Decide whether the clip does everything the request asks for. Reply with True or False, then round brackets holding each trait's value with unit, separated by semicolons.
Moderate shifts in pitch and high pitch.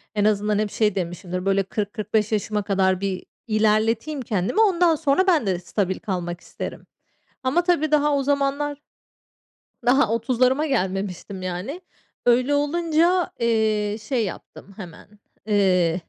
False (6.4 semitones; 215 Hz)